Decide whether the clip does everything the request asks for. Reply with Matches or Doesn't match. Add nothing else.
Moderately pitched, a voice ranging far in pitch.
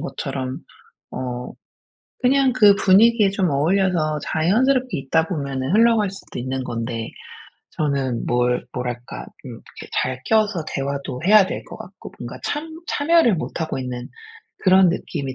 Matches